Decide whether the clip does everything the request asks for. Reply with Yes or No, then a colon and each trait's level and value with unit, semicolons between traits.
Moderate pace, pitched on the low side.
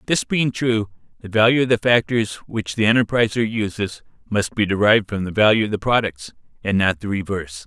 Yes: average, 195 wpm; low, 105 Hz